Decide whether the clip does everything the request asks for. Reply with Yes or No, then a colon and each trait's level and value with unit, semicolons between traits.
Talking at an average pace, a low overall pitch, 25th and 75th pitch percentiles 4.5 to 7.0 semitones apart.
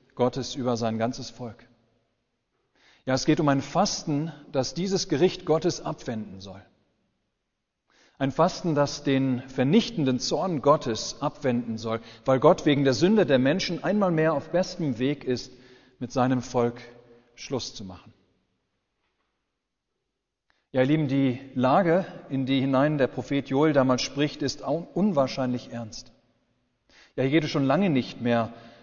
No: average, 145 wpm; low, 130 Hz; average, 3.7 semitones